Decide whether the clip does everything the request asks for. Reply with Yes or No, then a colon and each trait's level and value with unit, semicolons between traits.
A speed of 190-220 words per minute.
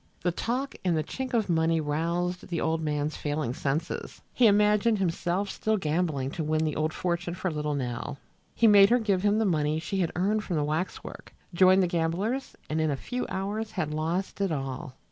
Yes: fast, 205 wpm